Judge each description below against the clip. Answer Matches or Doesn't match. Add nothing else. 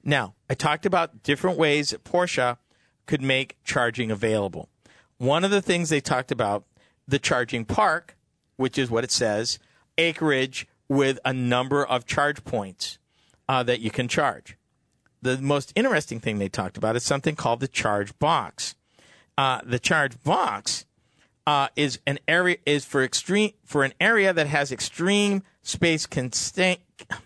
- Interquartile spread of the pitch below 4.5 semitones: Matches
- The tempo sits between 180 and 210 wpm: Doesn't match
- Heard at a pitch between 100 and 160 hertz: Matches